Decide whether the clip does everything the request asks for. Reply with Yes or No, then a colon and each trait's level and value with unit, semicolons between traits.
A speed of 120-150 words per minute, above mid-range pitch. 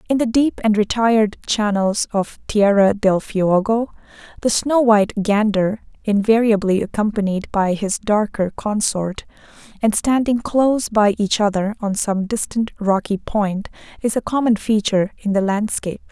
Yes: average, 140 wpm; high, 210 Hz